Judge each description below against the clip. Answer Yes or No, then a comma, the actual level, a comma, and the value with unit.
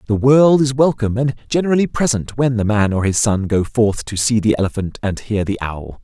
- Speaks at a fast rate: Yes, fast, 230 wpm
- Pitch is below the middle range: Yes, low, 115 Hz